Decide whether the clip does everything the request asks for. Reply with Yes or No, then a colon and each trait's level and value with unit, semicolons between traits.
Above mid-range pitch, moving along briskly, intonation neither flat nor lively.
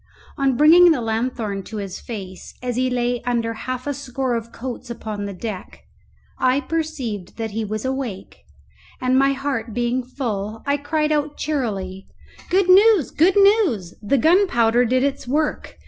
No: very high, 250 Hz; average, 160 wpm; average, 4.4 semitones